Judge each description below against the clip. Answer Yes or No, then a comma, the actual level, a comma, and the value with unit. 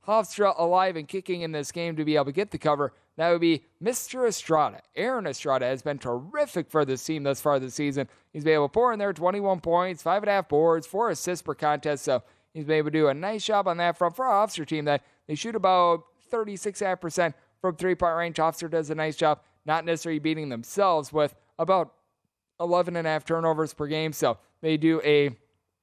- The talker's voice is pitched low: No, medium, 160 Hz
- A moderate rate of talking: No, fast, 220 wpm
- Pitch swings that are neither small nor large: Yes, average, 3.4 semitones